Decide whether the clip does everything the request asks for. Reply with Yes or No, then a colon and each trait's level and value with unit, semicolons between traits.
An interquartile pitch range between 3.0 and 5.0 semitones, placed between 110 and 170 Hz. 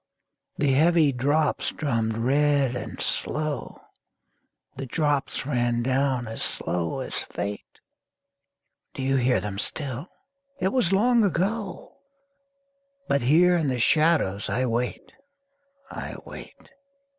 Yes: average, 4.6 semitones; low, 135 Hz